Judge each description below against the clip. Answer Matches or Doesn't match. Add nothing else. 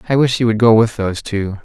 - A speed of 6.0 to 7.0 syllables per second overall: Matches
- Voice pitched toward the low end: Matches